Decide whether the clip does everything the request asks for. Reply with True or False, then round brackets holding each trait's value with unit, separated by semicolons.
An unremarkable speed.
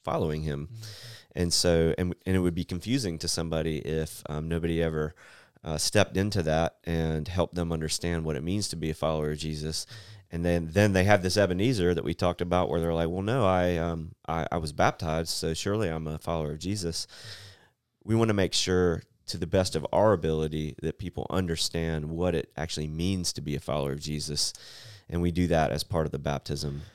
False (210 wpm)